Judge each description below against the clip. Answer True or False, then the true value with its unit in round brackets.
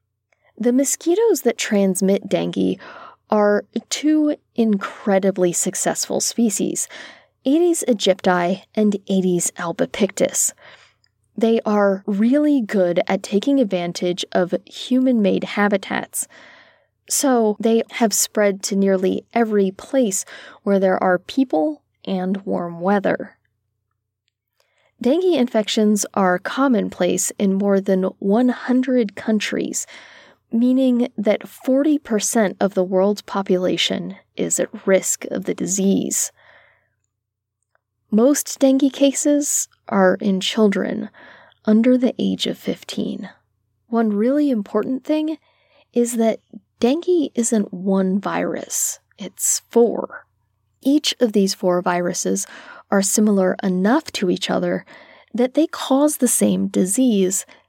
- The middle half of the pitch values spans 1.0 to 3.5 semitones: False (5.0 semitones)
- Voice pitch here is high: True (210 Hz)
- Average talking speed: False (105 wpm)